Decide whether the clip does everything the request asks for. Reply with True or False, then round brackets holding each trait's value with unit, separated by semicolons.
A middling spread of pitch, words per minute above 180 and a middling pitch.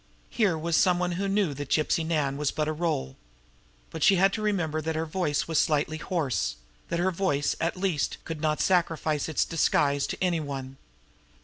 True (3.3 semitones; 195 wpm; 160 Hz)